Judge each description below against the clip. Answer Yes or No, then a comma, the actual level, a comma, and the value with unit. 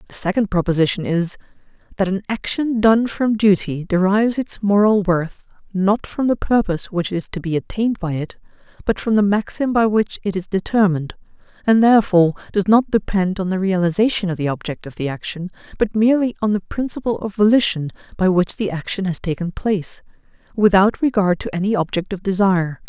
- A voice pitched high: Yes, high, 195 Hz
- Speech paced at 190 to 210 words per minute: No, average, 180 wpm